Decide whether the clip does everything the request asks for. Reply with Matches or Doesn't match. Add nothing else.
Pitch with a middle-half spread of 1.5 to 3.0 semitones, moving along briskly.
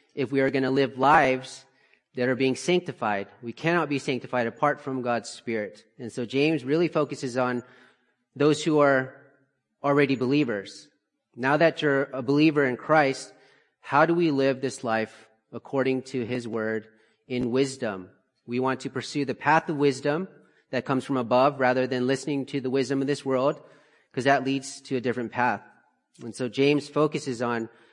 Doesn't match